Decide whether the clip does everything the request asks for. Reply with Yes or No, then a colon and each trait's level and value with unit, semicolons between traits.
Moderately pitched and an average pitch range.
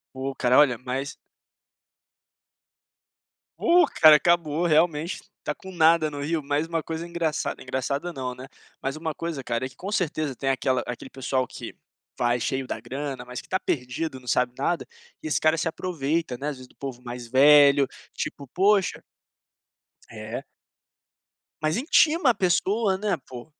Yes: medium, 150 Hz; average, 4.3 semitones